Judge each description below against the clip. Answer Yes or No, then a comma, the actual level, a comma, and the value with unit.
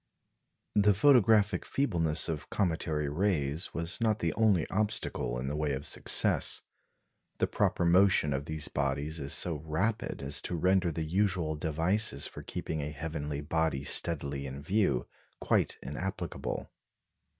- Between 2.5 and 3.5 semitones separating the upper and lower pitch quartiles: No, average, 4.8 semitones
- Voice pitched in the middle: No, very low, 80 Hz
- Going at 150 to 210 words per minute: No, average, 140 wpm